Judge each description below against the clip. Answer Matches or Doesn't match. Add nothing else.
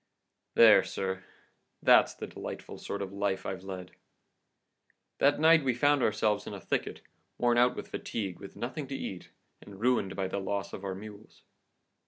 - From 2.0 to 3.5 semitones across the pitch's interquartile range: Doesn't match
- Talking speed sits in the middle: Matches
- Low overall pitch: Matches